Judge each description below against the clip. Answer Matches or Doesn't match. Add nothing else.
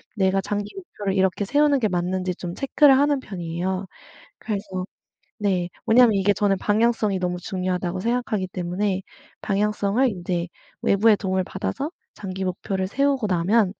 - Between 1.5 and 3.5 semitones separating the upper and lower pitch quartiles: Matches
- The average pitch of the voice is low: Doesn't match